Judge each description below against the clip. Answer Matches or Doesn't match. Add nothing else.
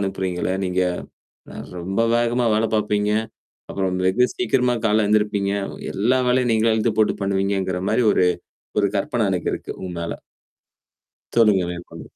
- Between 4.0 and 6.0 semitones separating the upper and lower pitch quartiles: Doesn't match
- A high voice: Doesn't match